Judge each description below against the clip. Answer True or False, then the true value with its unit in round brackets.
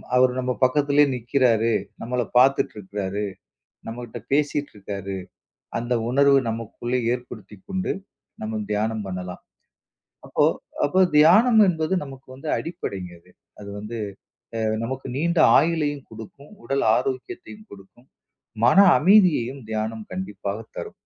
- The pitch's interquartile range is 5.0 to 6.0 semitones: True (5.3 semitones)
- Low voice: True (125 Hz)